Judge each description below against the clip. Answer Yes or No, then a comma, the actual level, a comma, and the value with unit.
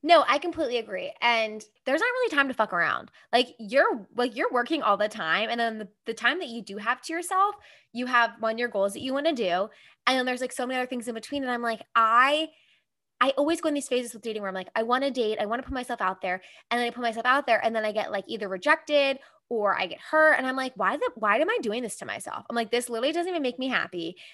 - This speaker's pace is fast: Yes, fast, 285 wpm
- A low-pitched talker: No, high, 245 Hz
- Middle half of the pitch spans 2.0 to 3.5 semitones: No, average, 4.2 semitones